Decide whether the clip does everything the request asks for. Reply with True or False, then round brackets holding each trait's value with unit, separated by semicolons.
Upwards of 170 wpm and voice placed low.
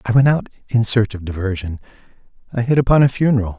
True (200 wpm; 115 Hz)